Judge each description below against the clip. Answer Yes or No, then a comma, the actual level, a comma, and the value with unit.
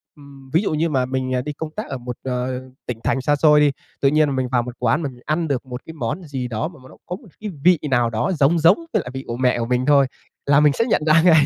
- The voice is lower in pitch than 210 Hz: Yes, medium, 140 Hz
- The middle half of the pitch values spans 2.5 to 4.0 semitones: Yes, average, 3.6 semitones